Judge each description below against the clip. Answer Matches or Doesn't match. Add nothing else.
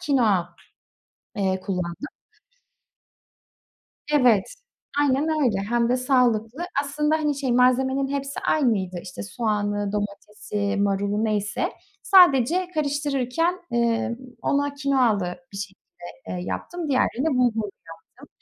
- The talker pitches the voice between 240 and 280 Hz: Matches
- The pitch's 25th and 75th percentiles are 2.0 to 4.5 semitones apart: Doesn't match